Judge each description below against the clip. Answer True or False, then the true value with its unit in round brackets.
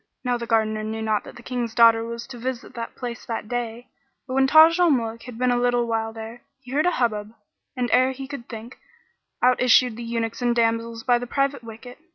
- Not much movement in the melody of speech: True (1.8 semitones)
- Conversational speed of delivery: False (225 wpm)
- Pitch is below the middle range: False (240 Hz)